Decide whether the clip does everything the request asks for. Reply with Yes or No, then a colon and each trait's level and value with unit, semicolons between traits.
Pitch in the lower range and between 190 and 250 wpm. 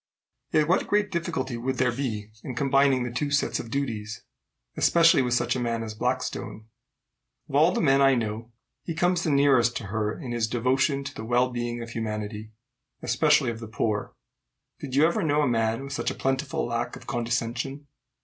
Yes: low, 125 Hz; average, 195 wpm